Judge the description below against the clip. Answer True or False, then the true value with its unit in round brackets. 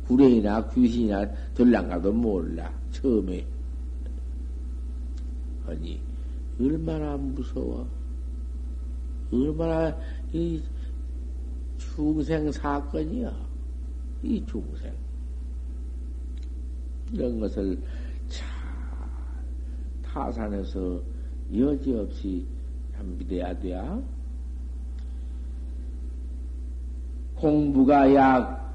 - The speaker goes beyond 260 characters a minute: False (125 characters per minute)